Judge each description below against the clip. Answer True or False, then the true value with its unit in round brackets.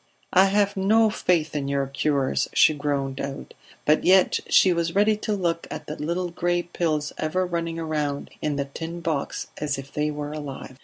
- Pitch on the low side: False (155 Hz)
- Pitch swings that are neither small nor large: True (3.4 semitones)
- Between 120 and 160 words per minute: False (190 wpm)